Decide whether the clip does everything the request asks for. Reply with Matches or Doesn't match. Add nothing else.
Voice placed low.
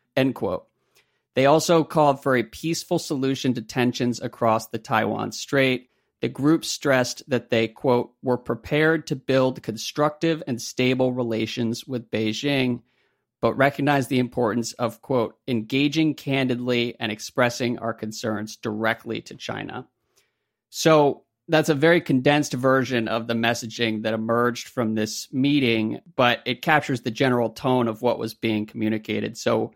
Matches